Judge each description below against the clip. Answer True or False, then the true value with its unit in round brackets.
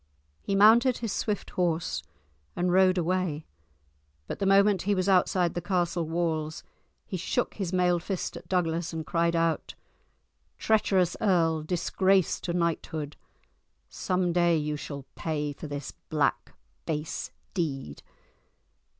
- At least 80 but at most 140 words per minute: True (135 wpm)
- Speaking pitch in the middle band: True (175 Hz)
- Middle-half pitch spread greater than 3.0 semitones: False (2.7 semitones)